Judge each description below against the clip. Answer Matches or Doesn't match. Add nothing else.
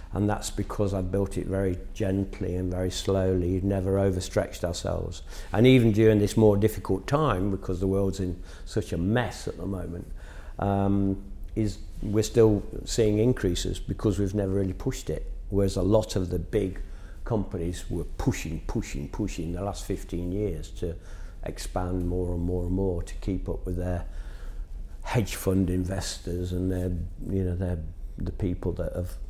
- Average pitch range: Doesn't match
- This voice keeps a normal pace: Matches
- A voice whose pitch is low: Matches